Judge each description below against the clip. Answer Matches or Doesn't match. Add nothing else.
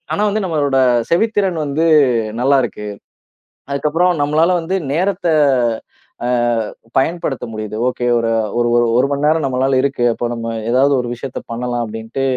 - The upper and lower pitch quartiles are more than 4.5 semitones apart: Matches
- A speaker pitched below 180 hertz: Matches